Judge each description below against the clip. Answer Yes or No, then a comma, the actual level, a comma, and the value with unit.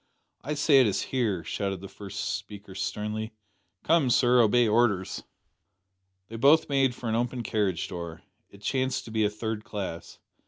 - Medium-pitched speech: No, low, 110 Hz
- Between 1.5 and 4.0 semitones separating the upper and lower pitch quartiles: Yes, average, 3.6 semitones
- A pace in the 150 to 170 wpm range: Yes, average, 165 wpm